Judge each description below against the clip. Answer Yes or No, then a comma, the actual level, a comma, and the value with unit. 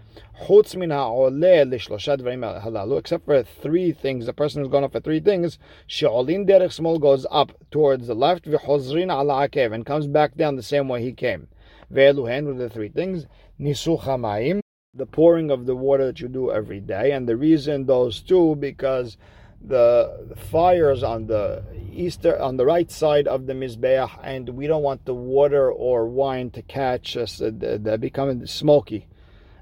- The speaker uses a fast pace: No, average, 155 wpm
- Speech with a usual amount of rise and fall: Yes, average, 3.9 semitones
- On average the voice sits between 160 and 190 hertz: No, low, 135 Hz